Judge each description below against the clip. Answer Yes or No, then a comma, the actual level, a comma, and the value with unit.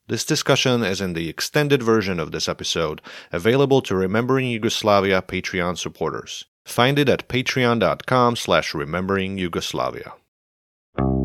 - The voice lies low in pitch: Yes, low, 105 Hz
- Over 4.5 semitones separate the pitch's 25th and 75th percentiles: Yes, wide, 5.4 semitones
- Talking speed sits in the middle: No, slow, 125 wpm